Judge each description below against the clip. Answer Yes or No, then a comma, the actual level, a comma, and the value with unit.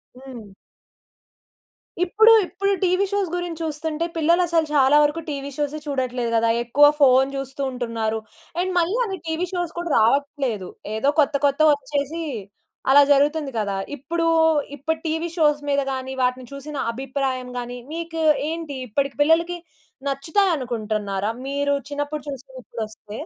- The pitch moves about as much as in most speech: Yes, average, 4.1 semitones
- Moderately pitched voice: No, very high, 285 Hz